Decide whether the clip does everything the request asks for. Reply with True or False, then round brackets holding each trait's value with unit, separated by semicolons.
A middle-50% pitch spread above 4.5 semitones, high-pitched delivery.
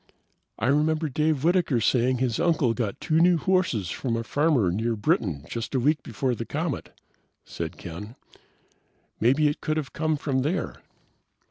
False (5.2 semitones; 135 Hz)